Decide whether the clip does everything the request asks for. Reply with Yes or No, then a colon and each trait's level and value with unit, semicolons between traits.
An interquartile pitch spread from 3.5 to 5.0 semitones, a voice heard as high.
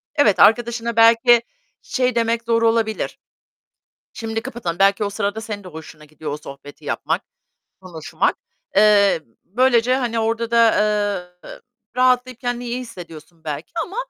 Yes: average, 3.9 semitones; high, 225 Hz